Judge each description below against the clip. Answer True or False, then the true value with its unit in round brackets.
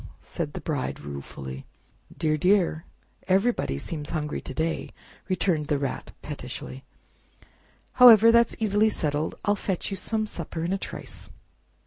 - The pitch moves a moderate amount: False (5.7 semitones)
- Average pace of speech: False (130 wpm)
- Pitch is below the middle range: False (165 Hz)